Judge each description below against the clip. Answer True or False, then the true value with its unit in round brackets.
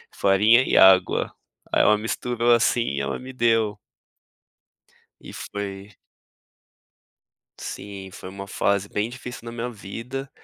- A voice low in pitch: True (105 Hz)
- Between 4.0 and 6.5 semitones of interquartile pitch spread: False (3.4 semitones)